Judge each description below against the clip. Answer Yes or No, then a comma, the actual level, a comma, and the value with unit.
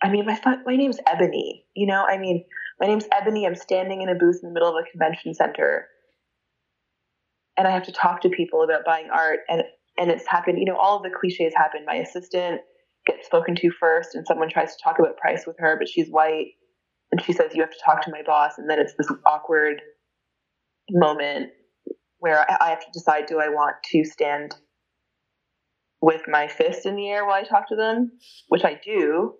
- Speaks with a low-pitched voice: No, medium, 185 Hz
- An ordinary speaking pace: No, fast, 210 wpm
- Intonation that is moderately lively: No, wide, 7.9 semitones